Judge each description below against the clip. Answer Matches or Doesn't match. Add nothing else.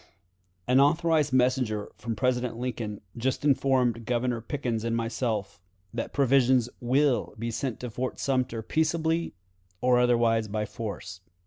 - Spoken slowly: Matches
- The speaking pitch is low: Matches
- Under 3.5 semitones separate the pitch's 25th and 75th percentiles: Matches